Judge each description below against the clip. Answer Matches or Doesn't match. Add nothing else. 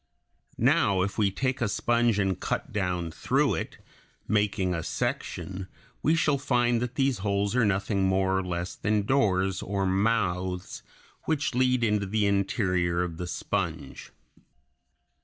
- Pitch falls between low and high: Doesn't match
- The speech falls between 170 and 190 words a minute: Doesn't match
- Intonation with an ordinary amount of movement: Matches